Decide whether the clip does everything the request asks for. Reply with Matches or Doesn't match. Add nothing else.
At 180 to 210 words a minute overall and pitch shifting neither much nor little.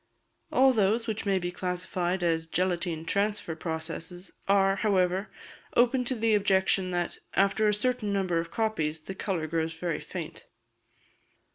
Doesn't match